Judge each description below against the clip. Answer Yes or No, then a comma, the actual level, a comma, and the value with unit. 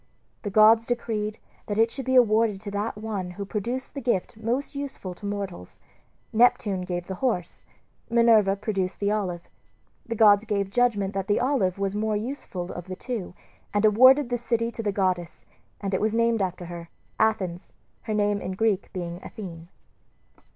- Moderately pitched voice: No, high, 210 Hz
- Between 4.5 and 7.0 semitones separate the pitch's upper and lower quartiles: No, average, 3.3 semitones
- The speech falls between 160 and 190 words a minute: Yes, average, 180 wpm